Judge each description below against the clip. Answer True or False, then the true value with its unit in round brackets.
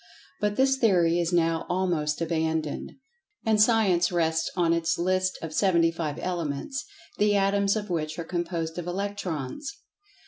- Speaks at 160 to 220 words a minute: False (145 wpm)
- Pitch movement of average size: True (3.3 semitones)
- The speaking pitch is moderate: True (175 Hz)